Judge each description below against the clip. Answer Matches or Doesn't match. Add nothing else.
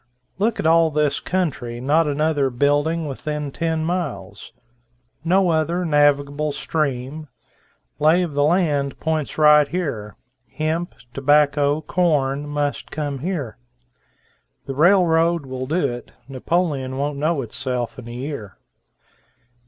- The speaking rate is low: Matches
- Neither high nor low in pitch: Matches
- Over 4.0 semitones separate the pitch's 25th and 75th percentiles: Doesn't match